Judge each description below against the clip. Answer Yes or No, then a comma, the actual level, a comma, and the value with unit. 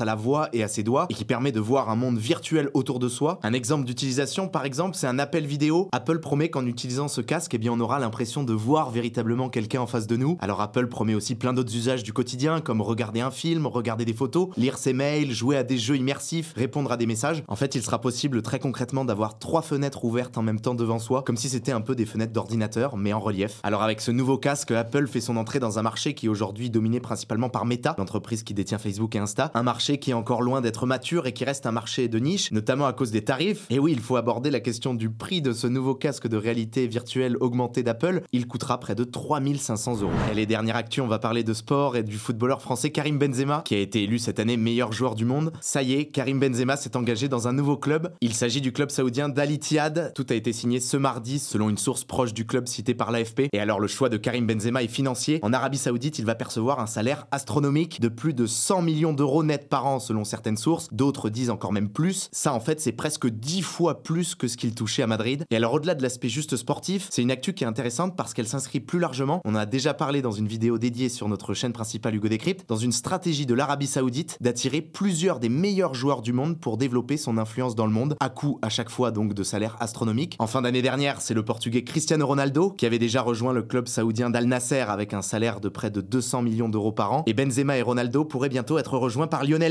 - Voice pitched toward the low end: Yes, low, 125 Hz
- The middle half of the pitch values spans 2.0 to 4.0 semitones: Yes, average, 3.6 semitones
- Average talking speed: No, fast, 255 wpm